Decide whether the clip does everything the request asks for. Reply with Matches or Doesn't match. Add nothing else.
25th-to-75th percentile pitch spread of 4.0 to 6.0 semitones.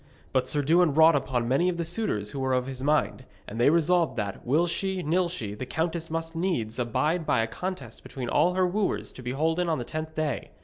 Matches